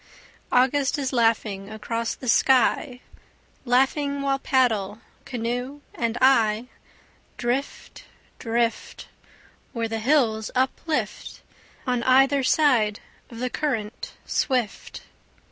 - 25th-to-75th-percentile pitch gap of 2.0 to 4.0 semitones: Yes, average, 3.0 semitones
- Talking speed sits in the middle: No, slow, 95 wpm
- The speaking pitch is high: Yes, high, 245 Hz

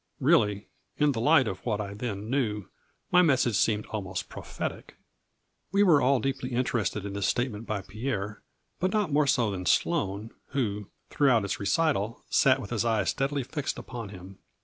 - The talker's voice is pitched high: No, low, 115 Hz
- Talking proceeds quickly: No, average, 175 wpm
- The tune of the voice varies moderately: Yes, average, 5.0 semitones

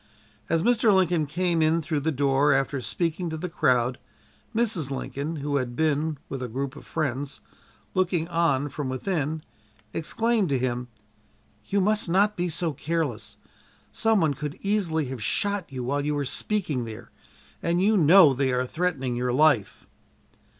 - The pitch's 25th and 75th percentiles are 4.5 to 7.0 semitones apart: Yes, average, 4.8 semitones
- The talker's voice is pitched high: No, medium, 155 Hz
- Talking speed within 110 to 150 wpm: No, average, 165 wpm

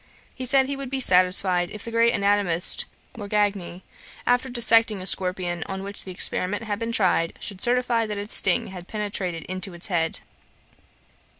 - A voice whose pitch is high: Yes, high, 200 Hz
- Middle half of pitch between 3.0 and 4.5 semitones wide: Yes, average, 4.0 semitones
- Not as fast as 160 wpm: No, average, 170 wpm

